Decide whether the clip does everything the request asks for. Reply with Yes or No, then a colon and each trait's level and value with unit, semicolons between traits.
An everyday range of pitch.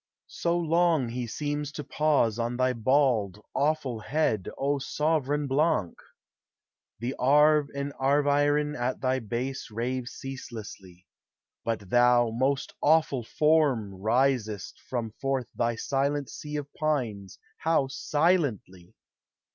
Yes: average, 4.0 semitones